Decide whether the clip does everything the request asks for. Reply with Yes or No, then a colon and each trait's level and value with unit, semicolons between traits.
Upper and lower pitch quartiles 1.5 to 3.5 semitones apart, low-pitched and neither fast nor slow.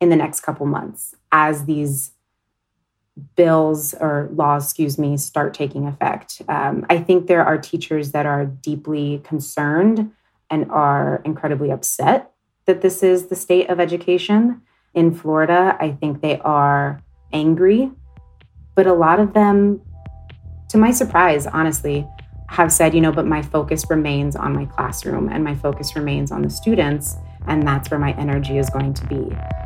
No: average, 3.1 semitones; medium, 150 Hz; average, 160 wpm